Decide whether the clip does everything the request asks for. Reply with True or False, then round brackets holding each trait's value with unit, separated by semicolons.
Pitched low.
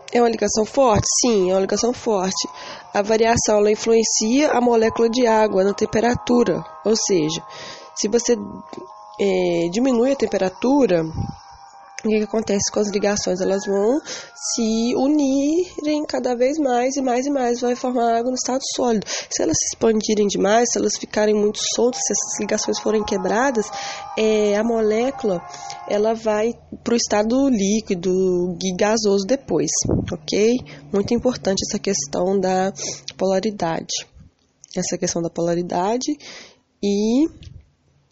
False (220 Hz)